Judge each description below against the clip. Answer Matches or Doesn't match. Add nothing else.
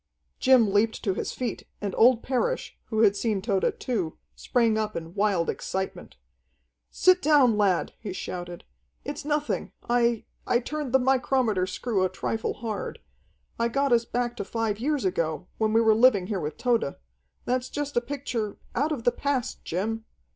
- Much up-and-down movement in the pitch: Doesn't match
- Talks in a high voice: Matches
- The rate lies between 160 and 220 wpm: Matches